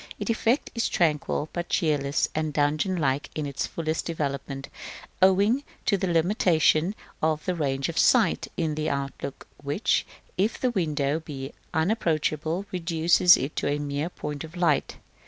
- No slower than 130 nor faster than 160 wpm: Yes, average, 155 wpm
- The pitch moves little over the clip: No, average, 3.6 semitones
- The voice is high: No, medium, 155 Hz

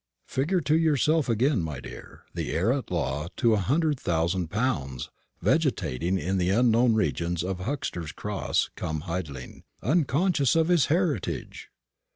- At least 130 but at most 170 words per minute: Yes, average, 145 wpm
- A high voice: No, low, 110 Hz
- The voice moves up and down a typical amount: No, wide, 8.8 semitones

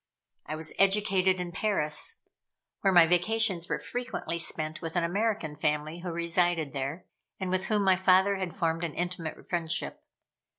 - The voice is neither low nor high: Yes, medium, 175 Hz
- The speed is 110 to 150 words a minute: No, average, 160 wpm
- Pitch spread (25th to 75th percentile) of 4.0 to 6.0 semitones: No, average, 2.8 semitones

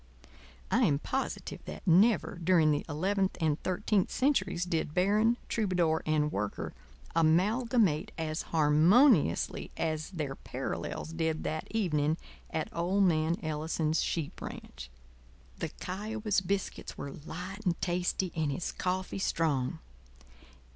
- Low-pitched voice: No, medium, 170 Hz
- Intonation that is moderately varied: Yes, average, 3.7 semitones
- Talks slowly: Yes, slow, 120 wpm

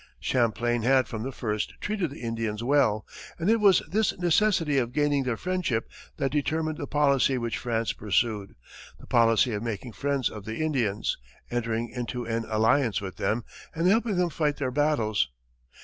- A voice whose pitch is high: No, low, 125 Hz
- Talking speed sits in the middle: Yes, average, 170 wpm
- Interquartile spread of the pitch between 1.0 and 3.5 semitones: No, average, 4.9 semitones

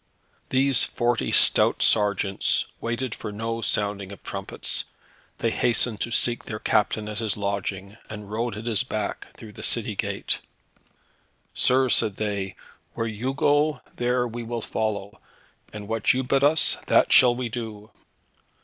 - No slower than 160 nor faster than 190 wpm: No, average, 150 wpm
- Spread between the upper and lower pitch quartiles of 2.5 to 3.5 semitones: Yes, average, 2.8 semitones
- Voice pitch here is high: No, low, 110 Hz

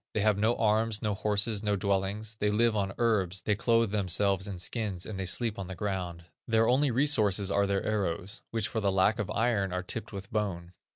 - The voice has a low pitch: Yes, low, 105 Hz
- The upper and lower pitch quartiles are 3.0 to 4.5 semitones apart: No, narrow, 2.4 semitones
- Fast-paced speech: Yes, fast, 215 wpm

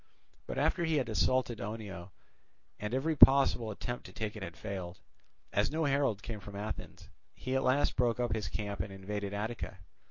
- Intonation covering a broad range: No, average, 4.1 semitones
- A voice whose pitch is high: No, low, 110 Hz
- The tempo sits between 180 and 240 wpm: Yes, average, 185 wpm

